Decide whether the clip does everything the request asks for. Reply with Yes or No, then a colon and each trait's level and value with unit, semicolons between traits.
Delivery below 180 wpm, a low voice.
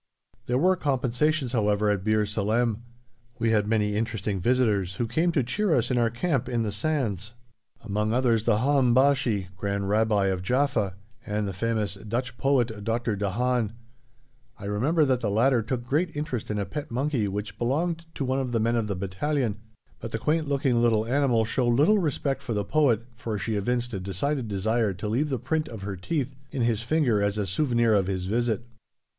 No: average, 195 wpm; low, 115 Hz